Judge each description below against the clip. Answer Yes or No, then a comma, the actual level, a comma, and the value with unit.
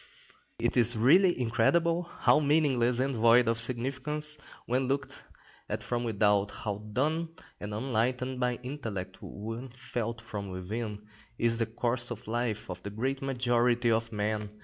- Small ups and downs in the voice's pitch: No, average, 3.1 semitones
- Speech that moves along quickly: No, average, 150 wpm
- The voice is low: Yes, low, 120 Hz